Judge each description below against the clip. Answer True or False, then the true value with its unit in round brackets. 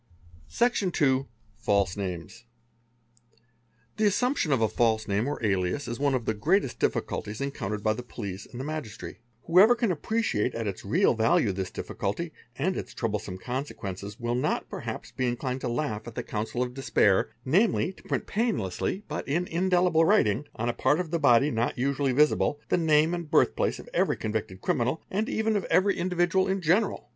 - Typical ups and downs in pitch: False (8.0 semitones)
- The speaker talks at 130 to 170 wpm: False (185 wpm)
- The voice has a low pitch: True (130 Hz)